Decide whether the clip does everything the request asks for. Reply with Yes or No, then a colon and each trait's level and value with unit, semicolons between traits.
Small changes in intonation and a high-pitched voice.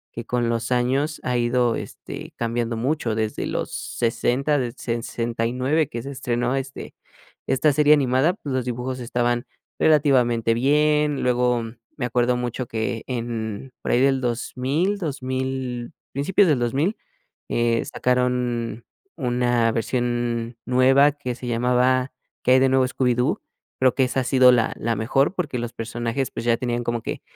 No: narrow, 2.0 semitones; low, 125 Hz